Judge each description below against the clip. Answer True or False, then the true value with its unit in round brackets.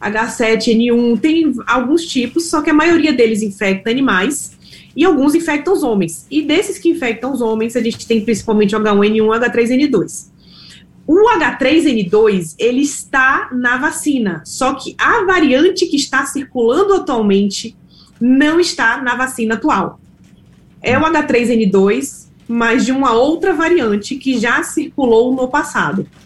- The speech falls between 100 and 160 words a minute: True (150 wpm)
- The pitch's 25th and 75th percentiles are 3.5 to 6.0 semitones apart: True (5.2 semitones)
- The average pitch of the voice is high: True (255 Hz)